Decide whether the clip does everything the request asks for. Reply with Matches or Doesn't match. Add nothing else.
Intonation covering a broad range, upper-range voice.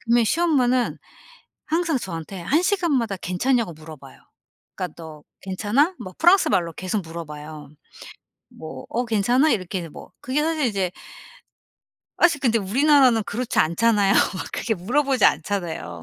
Matches